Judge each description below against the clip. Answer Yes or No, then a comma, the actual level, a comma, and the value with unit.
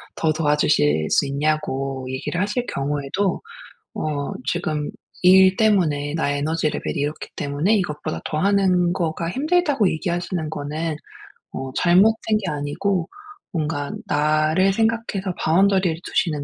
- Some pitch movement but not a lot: Yes, average, 4.5 semitones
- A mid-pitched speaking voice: Yes, medium, 160 Hz